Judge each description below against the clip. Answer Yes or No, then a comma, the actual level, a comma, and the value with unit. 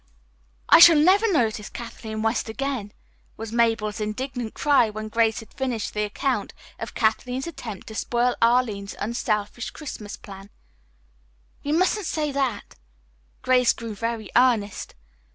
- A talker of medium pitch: No, high, 230 Hz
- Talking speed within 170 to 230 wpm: No, slow, 135 wpm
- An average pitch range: Yes, average, 3.6 semitones